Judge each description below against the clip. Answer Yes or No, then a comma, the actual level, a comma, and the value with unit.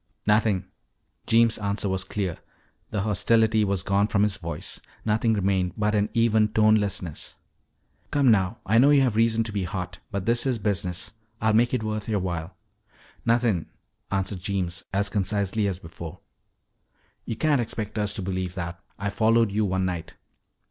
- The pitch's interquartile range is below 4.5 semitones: Yes, average, 2.8 semitones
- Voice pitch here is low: Yes, low, 105 Hz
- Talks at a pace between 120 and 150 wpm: No, average, 170 wpm